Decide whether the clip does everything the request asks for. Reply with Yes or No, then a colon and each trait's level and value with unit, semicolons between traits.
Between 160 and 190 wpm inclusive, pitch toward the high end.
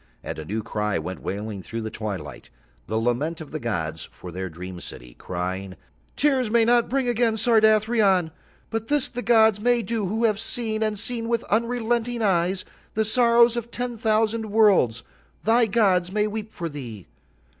Yes: average, 170 wpm; high, 215 Hz